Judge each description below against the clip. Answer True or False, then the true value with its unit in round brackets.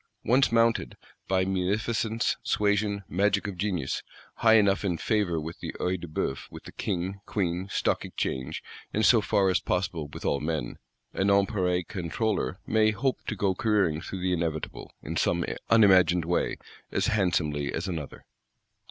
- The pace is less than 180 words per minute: True (160 wpm)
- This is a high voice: False (95 Hz)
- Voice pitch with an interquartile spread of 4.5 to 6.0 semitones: False (3.5 semitones)